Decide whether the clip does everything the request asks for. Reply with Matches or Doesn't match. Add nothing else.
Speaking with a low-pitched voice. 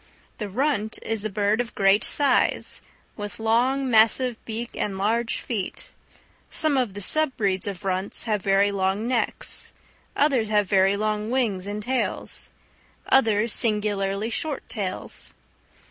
Doesn't match